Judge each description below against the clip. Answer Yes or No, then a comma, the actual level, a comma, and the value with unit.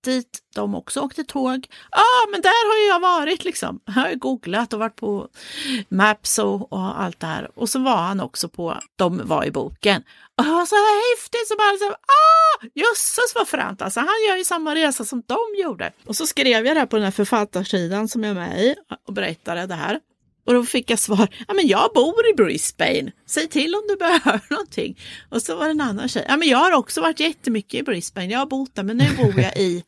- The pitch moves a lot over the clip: Yes, wide, 8.7 semitones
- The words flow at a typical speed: No, fast, 230 wpm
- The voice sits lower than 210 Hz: No, very high, 260 Hz